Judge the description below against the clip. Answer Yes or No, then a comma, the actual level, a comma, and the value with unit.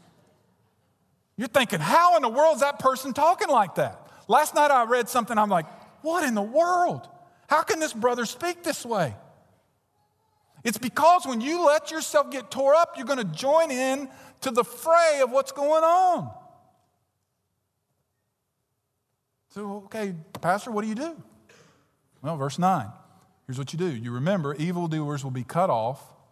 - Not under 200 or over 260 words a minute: No, average, 165 wpm